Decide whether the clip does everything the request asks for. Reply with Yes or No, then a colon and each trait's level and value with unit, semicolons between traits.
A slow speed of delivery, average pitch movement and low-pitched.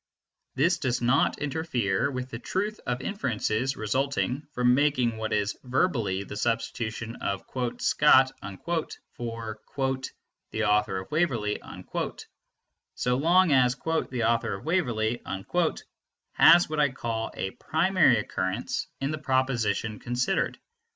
Yes: slow, 120 wpm; average, 4.5 semitones; low, 125 Hz